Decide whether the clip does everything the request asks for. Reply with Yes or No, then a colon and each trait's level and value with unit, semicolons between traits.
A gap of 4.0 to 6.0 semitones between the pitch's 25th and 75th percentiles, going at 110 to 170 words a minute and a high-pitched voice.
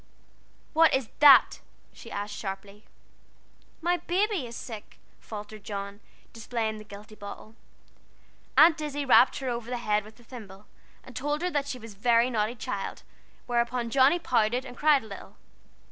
Yes: average, 4.5 semitones; average, 160 wpm; high, 235 Hz